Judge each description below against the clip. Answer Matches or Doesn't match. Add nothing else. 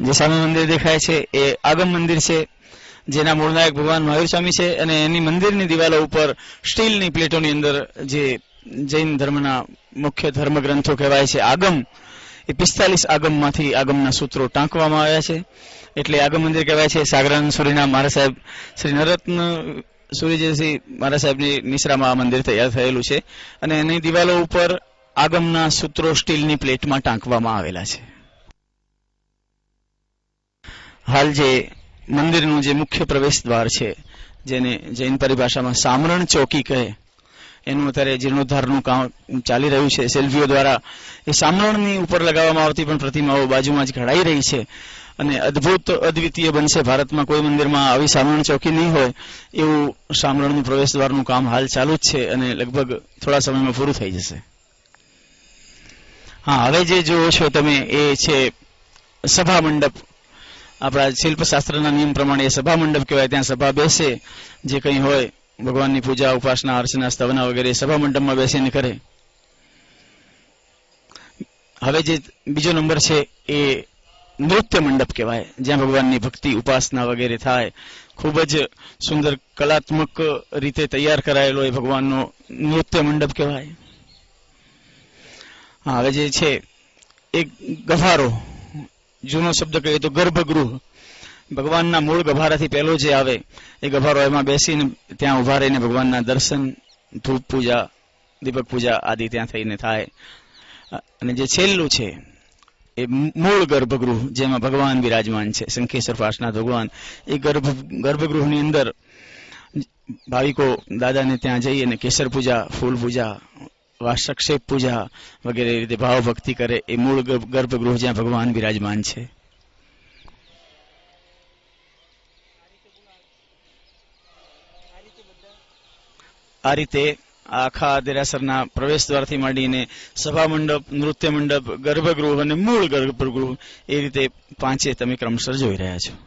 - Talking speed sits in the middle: Matches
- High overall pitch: Doesn't match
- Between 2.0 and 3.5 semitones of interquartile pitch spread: Matches